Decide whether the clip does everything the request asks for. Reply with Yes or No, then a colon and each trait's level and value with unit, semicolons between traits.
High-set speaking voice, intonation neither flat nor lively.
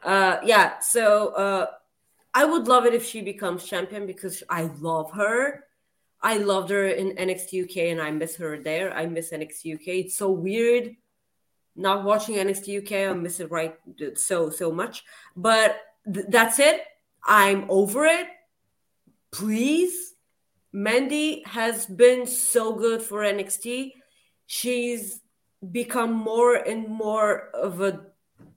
Yes: high, 205 Hz; average, 4.3 semitones